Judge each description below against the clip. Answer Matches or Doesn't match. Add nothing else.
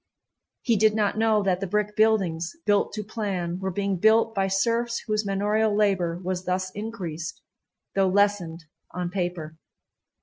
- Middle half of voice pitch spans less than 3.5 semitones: Matches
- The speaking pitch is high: Matches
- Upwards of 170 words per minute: Doesn't match